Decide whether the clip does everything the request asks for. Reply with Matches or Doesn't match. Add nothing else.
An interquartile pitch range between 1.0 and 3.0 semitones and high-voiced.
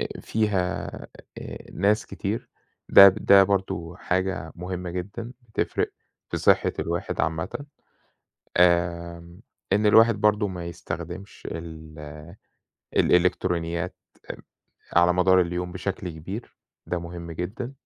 Doesn't match